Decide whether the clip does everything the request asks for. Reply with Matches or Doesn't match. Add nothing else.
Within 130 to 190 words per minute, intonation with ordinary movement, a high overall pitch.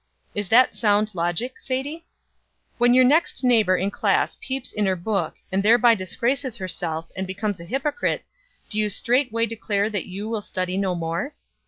Matches